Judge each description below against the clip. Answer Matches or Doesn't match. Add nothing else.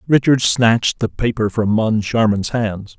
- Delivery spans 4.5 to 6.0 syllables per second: Doesn't match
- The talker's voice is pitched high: Doesn't match